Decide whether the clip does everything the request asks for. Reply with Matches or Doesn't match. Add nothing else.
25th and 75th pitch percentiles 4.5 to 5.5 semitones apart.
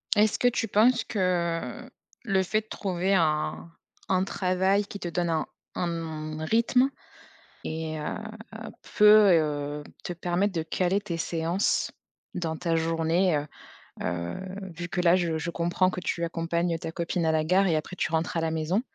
Doesn't match